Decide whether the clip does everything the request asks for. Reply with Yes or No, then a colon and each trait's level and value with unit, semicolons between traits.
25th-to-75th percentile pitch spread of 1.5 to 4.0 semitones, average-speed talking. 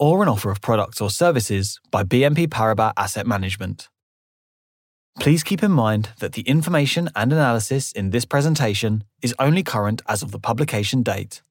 No: wide, 5.6 semitones; average, 165 wpm